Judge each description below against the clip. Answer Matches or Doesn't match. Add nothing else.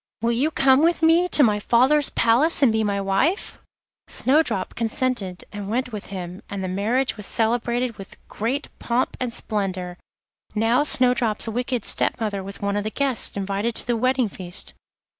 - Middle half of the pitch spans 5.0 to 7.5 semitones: Doesn't match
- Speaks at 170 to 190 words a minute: Matches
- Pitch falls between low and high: Doesn't match